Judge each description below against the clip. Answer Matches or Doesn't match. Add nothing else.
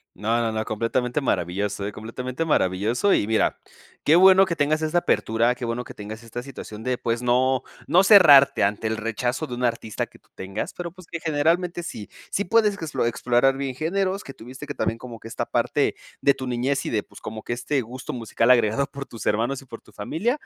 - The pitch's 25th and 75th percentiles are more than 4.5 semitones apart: Matches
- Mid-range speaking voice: Doesn't match